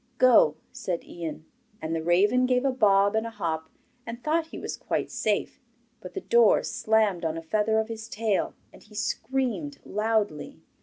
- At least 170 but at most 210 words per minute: Yes, average, 175 wpm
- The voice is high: Yes, high, 215 Hz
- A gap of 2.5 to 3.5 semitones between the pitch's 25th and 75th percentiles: No, average, 5.0 semitones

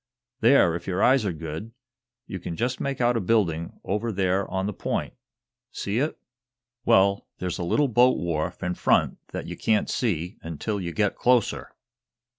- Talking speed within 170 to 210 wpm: Yes, average, 175 wpm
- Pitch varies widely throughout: No, average, 5.0 semitones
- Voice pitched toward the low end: Yes, low, 100 Hz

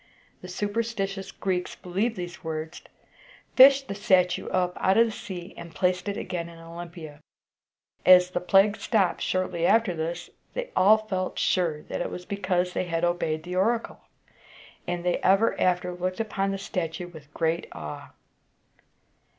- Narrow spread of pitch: Yes, narrow, 2.3 semitones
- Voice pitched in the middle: Yes, medium, 180 Hz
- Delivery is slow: No, average, 160 wpm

